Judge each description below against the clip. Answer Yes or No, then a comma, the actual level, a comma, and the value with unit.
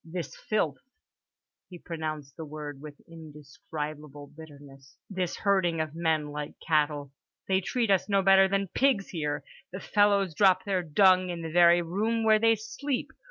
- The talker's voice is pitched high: No, medium, 170 Hz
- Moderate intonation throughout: Yes, average, 4.5 semitones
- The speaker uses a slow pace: No, average, 145 wpm